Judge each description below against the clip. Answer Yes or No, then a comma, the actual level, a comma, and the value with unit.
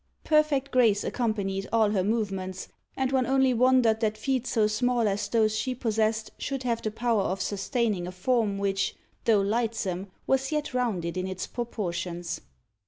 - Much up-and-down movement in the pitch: No, average, 4.1 semitones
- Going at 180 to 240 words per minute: No, average, 165 wpm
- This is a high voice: Yes, high, 220 Hz